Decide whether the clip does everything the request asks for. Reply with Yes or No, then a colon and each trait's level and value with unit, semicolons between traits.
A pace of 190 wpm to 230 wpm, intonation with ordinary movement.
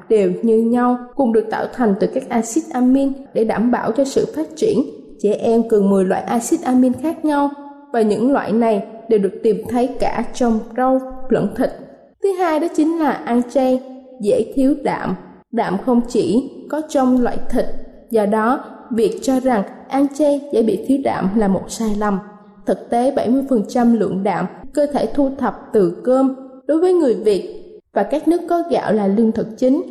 Yes: average, 195 wpm; average, 3.9 semitones